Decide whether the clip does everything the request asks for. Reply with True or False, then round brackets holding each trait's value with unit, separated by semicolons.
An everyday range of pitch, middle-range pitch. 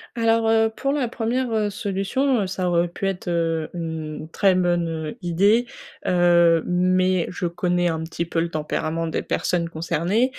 True (3.9 semitones; 175 Hz)